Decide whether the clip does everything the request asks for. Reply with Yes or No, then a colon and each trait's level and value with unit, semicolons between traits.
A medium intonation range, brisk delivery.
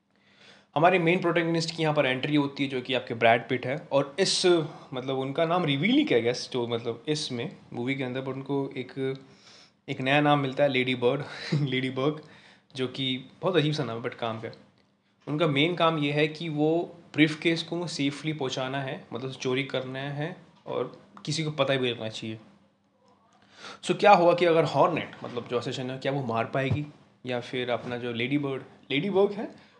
Yes: average, 3.8 semitones; fast, 200 wpm